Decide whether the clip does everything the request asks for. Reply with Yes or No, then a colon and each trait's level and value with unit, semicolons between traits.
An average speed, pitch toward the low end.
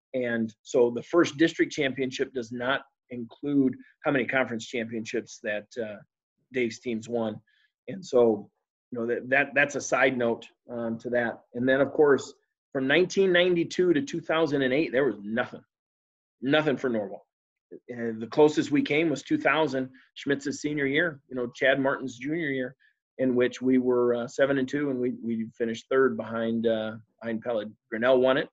Yes: average, 170 wpm; low, 130 Hz